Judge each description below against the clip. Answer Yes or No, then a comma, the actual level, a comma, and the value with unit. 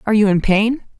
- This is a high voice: Yes, high, 215 Hz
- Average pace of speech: No, fast, 240 wpm